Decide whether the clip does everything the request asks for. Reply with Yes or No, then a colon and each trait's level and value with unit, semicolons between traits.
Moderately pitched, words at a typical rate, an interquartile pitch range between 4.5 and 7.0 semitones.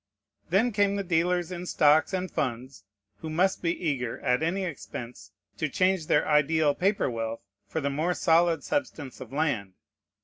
Yes: medium, 160 Hz; average, 165 wpm; average, 5.0 semitones